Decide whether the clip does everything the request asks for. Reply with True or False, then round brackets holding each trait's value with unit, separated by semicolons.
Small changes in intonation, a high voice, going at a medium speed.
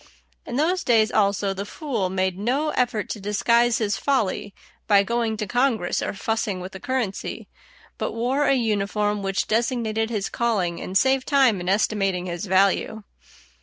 False (3.5 semitones; 215 Hz; 165 wpm)